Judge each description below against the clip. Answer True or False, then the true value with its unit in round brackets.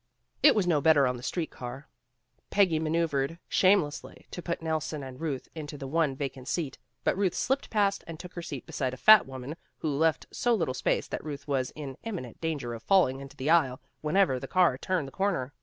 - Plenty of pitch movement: False (4.6 semitones)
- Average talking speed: False (210 wpm)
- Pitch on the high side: False (155 Hz)